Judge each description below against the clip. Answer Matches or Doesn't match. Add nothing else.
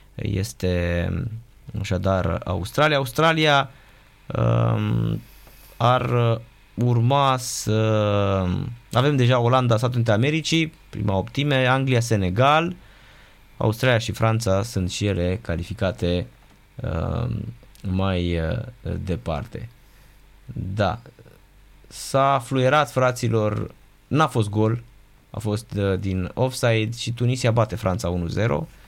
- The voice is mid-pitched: Doesn't match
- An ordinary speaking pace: Doesn't match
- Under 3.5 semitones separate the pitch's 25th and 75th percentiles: Doesn't match